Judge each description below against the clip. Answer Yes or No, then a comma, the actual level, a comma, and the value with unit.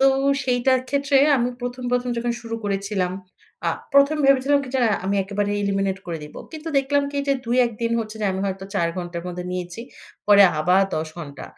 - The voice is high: Yes, high, 215 Hz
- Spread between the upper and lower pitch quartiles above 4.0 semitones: Yes, wide, 5.6 semitones